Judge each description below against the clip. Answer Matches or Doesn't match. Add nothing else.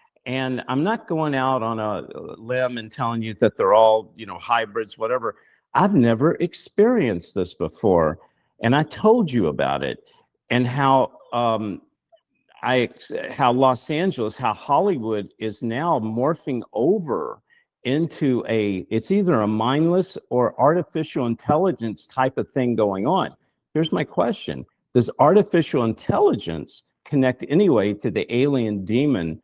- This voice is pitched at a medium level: Doesn't match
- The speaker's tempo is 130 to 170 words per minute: Matches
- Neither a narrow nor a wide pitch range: Doesn't match